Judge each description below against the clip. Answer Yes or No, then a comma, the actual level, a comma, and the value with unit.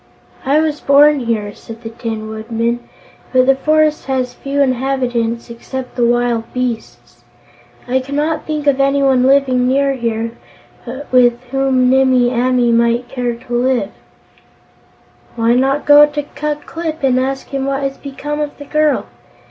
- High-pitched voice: Yes, very high, 260 Hz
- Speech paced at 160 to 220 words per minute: No, average, 150 wpm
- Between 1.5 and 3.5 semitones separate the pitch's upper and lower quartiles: Yes, average, 2.7 semitones